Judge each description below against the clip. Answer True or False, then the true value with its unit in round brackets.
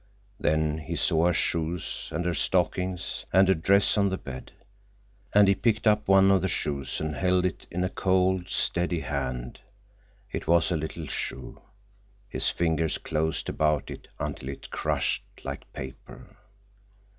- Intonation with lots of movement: False (3.5 semitones)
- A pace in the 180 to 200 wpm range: False (155 wpm)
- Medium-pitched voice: False (85 Hz)